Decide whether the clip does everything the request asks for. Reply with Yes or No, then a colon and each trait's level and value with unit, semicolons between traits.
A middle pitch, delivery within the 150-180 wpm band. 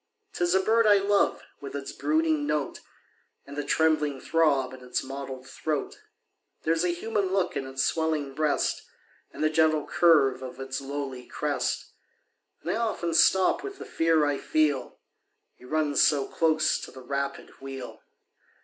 Yes: medium, 150 Hz; average, 165 wpm